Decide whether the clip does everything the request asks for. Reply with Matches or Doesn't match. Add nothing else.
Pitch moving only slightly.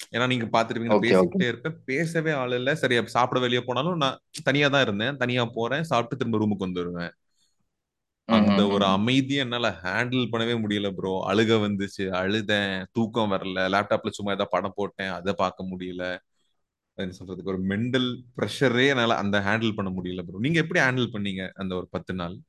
Doesn't match